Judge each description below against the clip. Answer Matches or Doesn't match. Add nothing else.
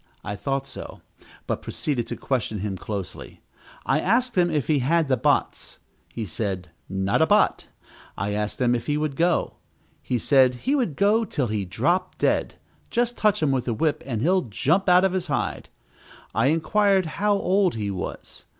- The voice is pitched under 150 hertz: Matches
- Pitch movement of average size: Doesn't match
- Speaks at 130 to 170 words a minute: Doesn't match